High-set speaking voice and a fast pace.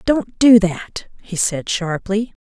No: high, 205 Hz; average, 150 wpm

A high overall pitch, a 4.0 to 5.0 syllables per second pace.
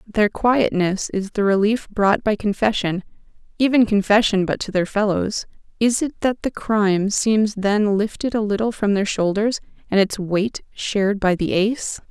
Yes: high, 210 Hz; 4.5 syllables/s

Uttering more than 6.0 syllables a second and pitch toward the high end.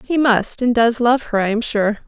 No: 4.8 syllables/s; high, 230 Hz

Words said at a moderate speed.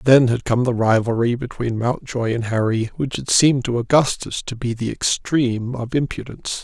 Yes: average, 180 wpm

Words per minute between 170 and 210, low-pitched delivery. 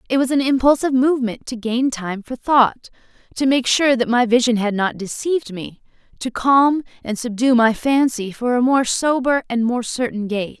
No: average, 180 wpm; high, 245 Hz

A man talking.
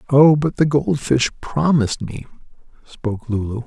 Yes: male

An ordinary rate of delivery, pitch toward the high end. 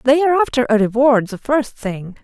No: fast, 215 wpm; very high, 250 Hz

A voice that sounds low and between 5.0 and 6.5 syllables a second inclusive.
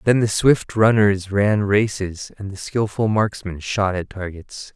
No: low, 100 Hz; 3.9 syllables/s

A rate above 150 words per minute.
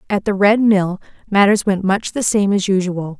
Yes: fast, 205 wpm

